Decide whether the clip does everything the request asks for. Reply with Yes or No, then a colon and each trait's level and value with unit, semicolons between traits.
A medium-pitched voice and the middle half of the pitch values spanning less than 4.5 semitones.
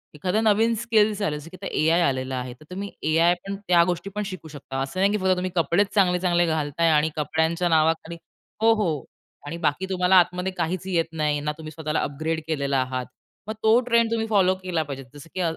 Yes: medium, 170 Hz; average, 3.8 semitones